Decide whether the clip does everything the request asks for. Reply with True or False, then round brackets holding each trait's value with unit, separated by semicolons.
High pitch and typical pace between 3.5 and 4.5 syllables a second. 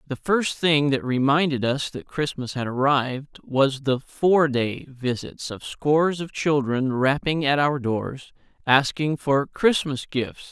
False (140 Hz; 4.0 syllables/s)